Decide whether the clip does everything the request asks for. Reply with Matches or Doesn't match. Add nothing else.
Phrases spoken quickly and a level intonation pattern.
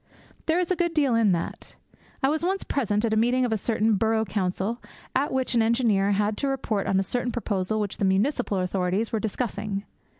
Doesn't match